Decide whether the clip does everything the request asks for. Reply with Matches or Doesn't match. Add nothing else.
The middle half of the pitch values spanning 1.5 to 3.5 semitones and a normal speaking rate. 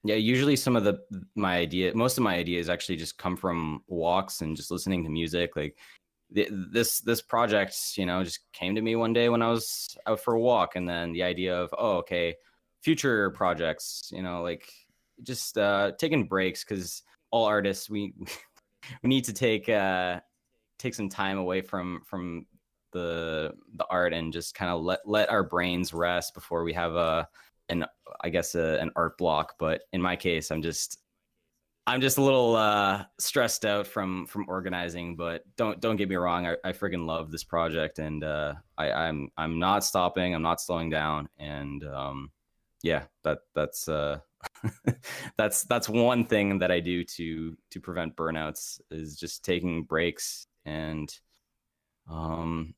Doesn't match